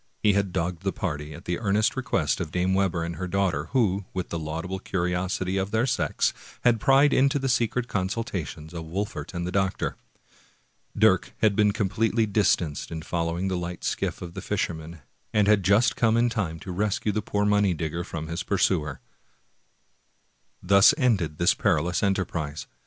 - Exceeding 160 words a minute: Yes, average, 180 wpm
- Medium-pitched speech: No, very low, 95 Hz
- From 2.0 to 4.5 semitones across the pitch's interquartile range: Yes, average, 3.7 semitones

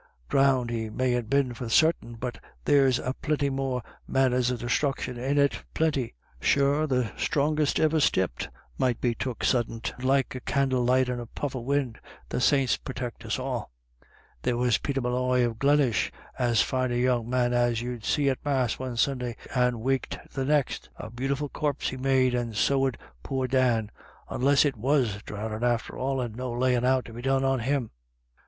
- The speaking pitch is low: Yes, low, 125 Hz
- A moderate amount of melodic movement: No, narrow, 2.2 semitones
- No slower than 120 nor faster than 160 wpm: No, average, 190 wpm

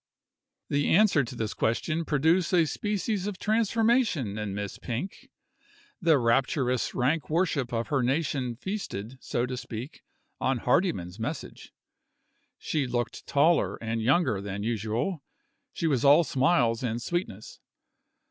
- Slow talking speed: Yes, slow, 130 wpm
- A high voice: No, low, 135 Hz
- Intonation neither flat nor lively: No, wide, 6.3 semitones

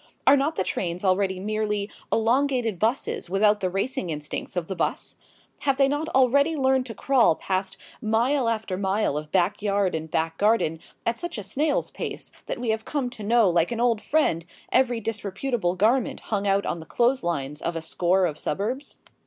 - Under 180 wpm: No, average, 185 wpm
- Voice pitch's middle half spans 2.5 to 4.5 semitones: No, average, 5.3 semitones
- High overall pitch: Yes, high, 210 Hz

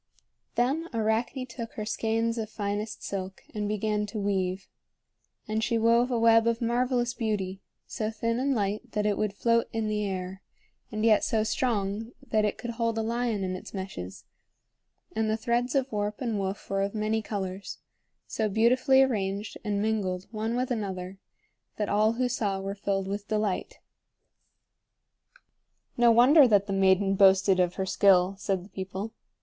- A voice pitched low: No, high, 215 Hz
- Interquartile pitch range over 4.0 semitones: No, average, 2.8 semitones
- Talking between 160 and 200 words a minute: Yes, average, 170 wpm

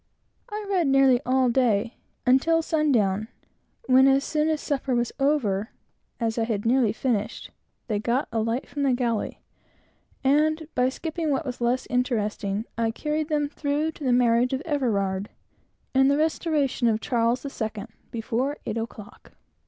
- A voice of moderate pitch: No, very high, 255 Hz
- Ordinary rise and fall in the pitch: Yes, average, 4.2 semitones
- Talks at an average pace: Yes, average, 160 wpm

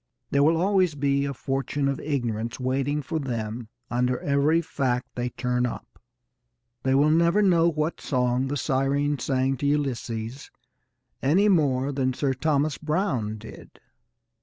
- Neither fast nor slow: Yes, average, 145 wpm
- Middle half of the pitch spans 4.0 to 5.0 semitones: No, average, 3.2 semitones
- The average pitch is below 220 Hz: Yes, medium, 140 Hz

